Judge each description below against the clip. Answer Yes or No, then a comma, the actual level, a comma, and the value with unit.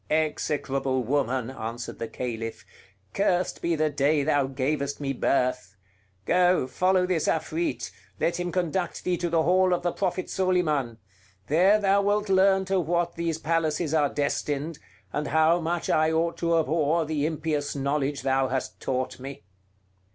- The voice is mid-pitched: Yes, medium, 155 Hz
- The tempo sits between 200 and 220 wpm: No, average, 155 wpm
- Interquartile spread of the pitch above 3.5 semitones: Yes, average, 4.1 semitones